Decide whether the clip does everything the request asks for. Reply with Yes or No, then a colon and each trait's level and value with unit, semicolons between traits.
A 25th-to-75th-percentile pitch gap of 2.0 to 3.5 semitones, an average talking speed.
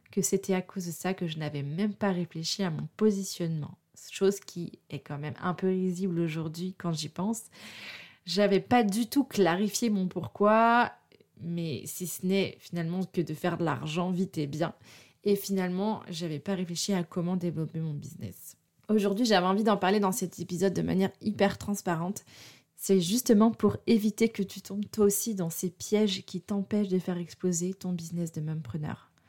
Yes: average, 2.9 semitones; average, 190 wpm